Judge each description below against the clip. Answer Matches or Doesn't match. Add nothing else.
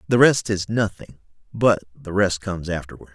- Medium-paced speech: Matches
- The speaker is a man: Matches